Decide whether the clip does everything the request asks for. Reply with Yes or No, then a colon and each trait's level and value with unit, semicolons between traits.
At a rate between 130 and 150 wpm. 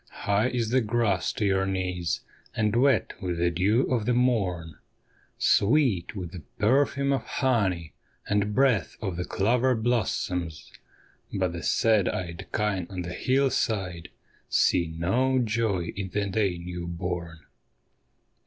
Yes: slow, 135 wpm